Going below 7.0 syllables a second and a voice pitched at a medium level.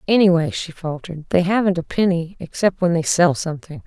Yes: 5.8 syllables/s; medium, 175 Hz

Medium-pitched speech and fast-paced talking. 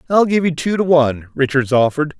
Yes: medium, 150 Hz; fast, 220 wpm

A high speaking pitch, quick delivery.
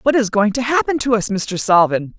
Yes: high, 215 Hz; fast, 245 wpm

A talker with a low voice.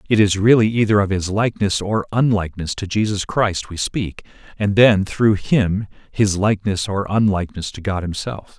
Yes: low, 100 Hz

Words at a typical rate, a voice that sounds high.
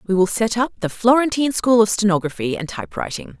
Yes: average, 195 wpm; high, 210 Hz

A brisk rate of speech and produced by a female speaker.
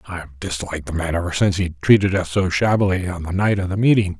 No: fast, 255 wpm; male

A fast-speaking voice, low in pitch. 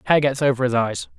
Yes: fast, 255 wpm; low, 130 Hz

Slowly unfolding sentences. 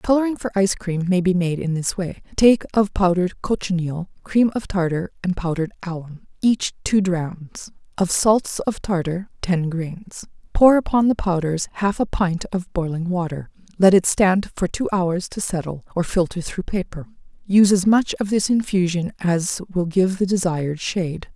No: average, 175 wpm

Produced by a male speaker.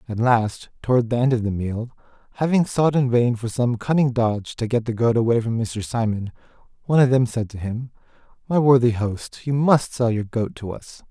Yes: male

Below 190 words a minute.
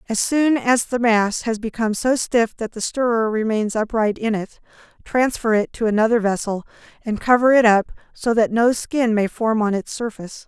No: average, 195 wpm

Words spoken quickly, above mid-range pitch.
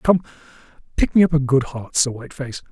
No: fast, 220 wpm; low, 135 Hz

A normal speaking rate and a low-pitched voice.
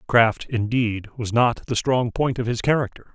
Yes: average, 190 wpm; low, 120 Hz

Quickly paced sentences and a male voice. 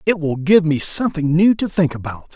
Yes: fast, 230 wpm; male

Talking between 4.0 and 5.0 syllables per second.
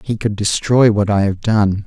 Yes: 4.5 syllables/s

